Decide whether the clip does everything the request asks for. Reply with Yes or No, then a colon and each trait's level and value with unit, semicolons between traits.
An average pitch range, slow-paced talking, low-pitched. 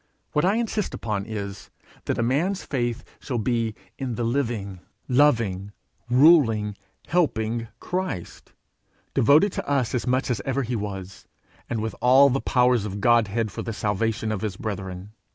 No: average, 4.2 semitones; average, 160 wpm; low, 115 Hz